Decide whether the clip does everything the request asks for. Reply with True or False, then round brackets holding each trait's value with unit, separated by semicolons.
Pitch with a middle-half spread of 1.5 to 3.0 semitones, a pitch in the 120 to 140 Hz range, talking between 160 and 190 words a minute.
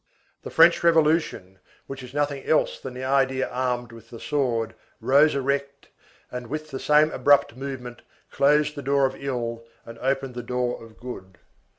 True (2.6 semitones; 135 Hz; 170 wpm)